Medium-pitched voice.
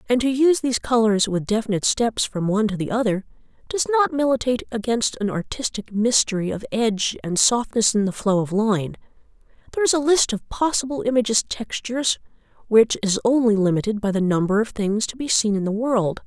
No: high, 225 Hz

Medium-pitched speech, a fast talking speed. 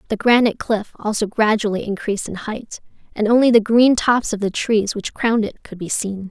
No: high, 215 Hz; fast, 210 wpm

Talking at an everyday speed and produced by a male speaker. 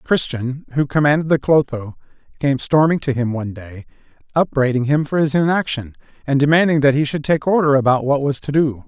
Yes: average, 190 wpm; male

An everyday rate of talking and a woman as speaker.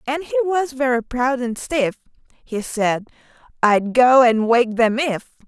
Yes: average, 165 wpm; female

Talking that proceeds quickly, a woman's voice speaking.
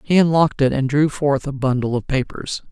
Yes: fast, 220 wpm; female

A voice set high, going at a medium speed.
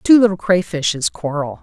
No: medium, 165 Hz; average, 145 wpm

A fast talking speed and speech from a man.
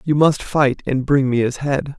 Yes: fast, 240 wpm; male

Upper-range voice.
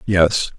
No: very low, 90 Hz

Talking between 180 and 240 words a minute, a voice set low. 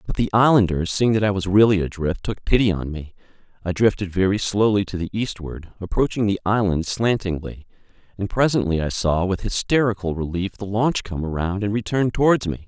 Yes: average, 185 wpm; low, 100 Hz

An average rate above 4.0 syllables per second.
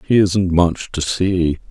No: 3.4 syllables/s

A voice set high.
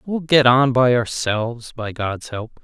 No: low, 120 Hz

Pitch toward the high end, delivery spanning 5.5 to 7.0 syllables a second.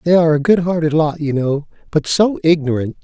No: medium, 160 Hz; 5.8 syllables/s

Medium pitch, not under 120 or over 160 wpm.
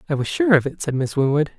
No: medium, 155 Hz; fast, 300 wpm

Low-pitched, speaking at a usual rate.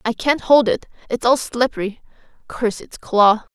No: high, 235 Hz; average, 170 wpm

